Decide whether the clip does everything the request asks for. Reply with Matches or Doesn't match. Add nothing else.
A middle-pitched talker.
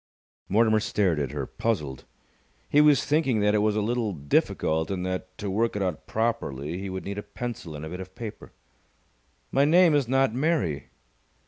Doesn't match